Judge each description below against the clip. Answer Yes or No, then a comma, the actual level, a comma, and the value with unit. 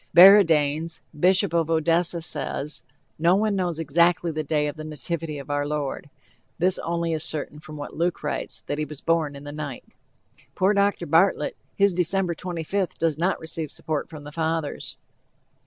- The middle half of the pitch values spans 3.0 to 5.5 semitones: No, narrow, 2.5 semitones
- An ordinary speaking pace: Yes, average, 170 wpm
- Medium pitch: Yes, medium, 160 Hz